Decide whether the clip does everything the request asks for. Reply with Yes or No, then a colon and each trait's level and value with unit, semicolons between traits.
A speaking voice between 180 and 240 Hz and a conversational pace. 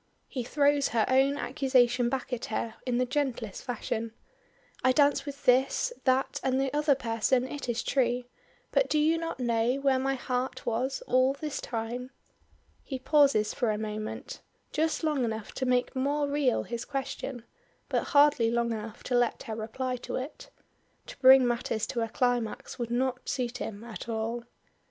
No: very high, 255 Hz; average, 175 wpm